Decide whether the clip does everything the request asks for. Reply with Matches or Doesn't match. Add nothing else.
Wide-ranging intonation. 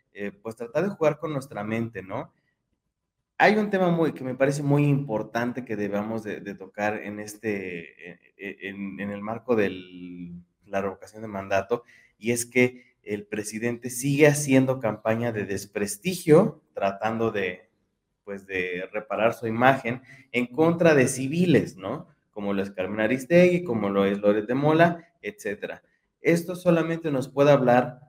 Matches